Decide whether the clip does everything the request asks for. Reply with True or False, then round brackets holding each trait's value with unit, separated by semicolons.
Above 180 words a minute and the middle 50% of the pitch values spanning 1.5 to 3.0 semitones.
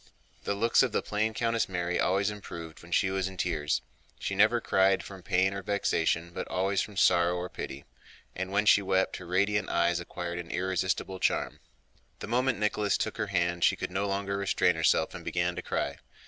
True (200 wpm; 2.6 semitones)